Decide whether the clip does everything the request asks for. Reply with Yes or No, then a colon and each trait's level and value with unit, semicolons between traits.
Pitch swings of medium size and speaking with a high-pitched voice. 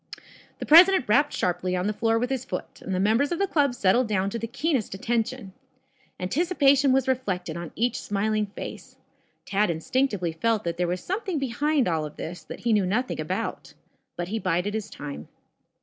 No: wide, 6.3 semitones; high, 220 Hz